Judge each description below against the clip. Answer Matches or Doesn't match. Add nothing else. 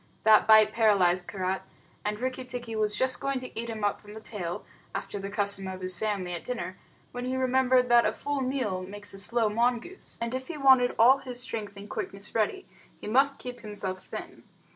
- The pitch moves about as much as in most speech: Matches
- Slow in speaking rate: Doesn't match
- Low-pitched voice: Doesn't match